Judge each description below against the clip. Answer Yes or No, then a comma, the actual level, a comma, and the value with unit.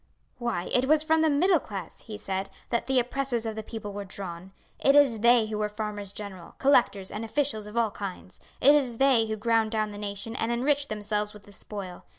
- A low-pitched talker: No, high, 220 Hz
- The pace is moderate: No, fast, 215 wpm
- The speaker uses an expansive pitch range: No, average, 3.6 semitones